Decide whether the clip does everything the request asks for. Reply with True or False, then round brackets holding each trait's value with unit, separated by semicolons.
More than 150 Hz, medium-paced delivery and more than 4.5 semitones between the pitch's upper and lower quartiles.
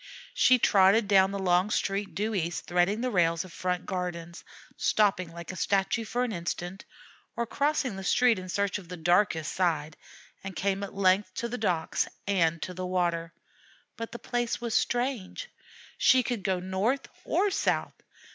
False (190 Hz; 175 wpm; 3.9 semitones)